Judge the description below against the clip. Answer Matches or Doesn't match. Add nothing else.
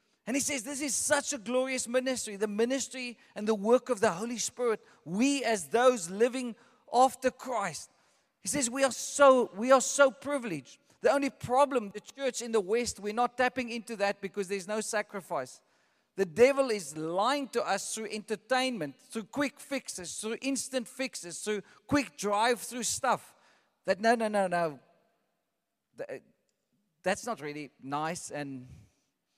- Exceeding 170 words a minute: Doesn't match